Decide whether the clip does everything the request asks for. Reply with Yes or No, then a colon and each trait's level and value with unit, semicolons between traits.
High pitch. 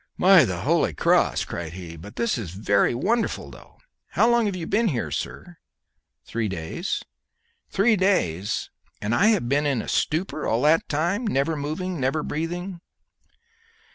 No: medium, 155 Hz